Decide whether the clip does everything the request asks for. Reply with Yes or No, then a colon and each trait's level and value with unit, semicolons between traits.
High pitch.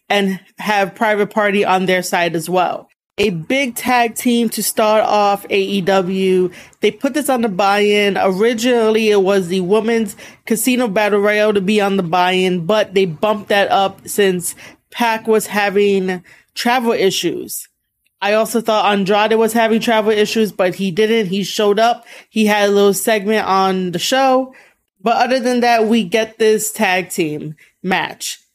Yes: high, 210 Hz